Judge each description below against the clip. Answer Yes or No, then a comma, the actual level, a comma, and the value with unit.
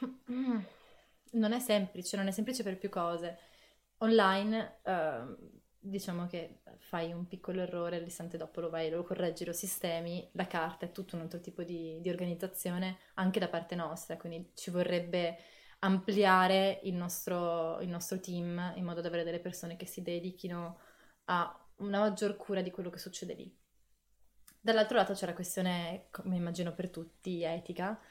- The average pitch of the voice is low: No, medium, 180 Hz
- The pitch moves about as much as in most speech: No, narrow, 2.2 semitones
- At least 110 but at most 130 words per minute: No, average, 165 wpm